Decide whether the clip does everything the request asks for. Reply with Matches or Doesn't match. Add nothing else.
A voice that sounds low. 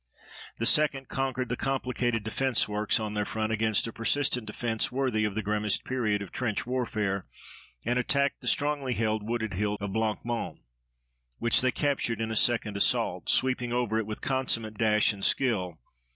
Matches